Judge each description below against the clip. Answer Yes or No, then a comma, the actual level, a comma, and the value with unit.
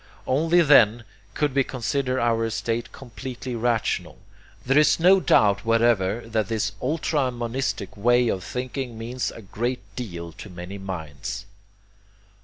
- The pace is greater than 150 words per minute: No, slow, 135 wpm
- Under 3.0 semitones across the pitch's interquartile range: No, average, 3.9 semitones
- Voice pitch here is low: Yes, low, 120 Hz